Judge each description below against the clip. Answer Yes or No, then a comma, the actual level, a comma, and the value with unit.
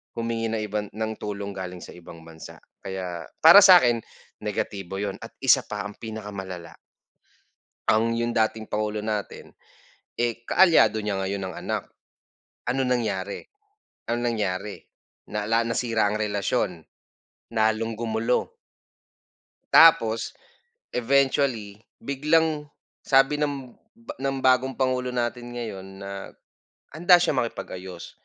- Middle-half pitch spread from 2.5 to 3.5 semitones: No, average, 3.9 semitones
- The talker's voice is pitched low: Yes, low, 110 Hz